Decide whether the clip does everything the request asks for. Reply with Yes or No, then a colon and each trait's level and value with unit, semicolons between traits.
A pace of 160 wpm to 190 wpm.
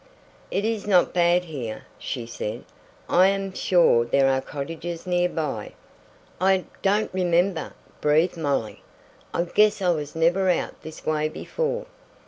No: average, 140 wpm